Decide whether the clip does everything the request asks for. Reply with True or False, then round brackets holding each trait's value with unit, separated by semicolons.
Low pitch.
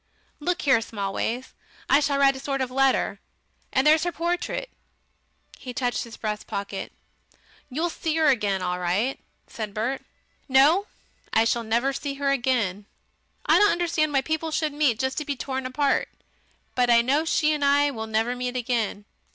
False (265 Hz)